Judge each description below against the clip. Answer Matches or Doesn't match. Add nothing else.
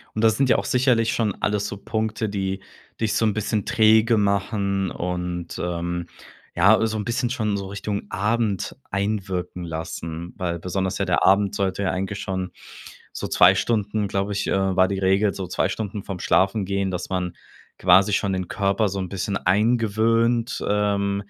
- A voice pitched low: Matches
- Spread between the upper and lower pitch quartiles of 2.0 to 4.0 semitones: Matches